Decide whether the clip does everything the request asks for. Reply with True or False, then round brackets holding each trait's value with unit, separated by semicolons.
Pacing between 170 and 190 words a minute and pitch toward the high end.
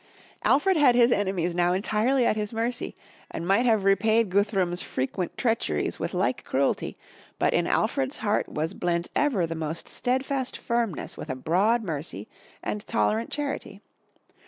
False (155 wpm; 205 Hz)